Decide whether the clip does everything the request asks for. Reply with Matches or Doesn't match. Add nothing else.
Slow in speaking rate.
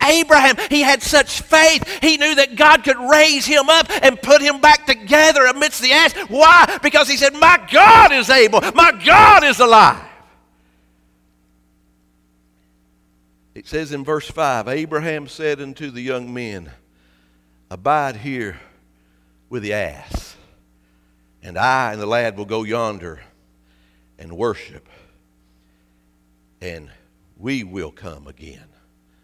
Matches